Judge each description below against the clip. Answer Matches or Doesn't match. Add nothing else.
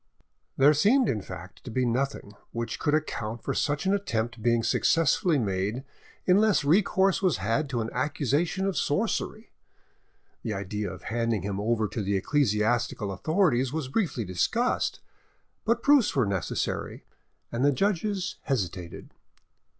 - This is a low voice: Matches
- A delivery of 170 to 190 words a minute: Doesn't match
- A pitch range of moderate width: Doesn't match